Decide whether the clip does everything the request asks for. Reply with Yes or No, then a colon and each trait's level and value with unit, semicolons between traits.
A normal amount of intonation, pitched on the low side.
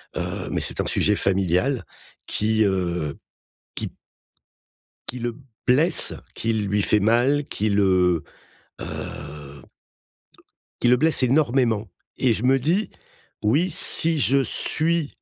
No: wide, 6.0 semitones; low, 115 Hz